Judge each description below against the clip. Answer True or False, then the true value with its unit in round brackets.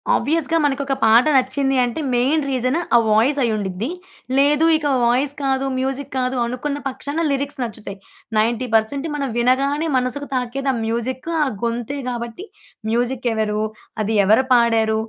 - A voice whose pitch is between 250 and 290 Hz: True (255 Hz)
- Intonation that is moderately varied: True (3.1 semitones)